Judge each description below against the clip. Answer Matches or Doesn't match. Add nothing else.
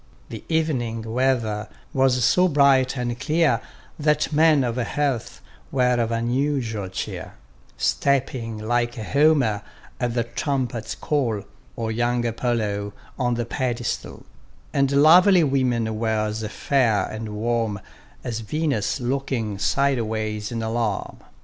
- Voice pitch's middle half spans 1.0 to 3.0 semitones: Doesn't match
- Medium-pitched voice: Doesn't match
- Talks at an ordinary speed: Doesn't match